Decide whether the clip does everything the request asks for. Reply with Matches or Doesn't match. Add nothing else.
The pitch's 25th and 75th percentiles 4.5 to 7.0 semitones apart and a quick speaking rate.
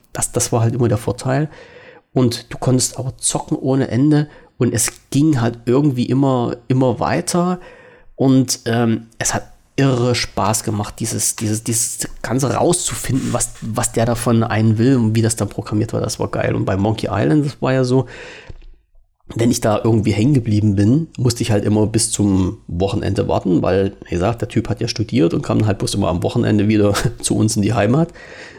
Doesn't match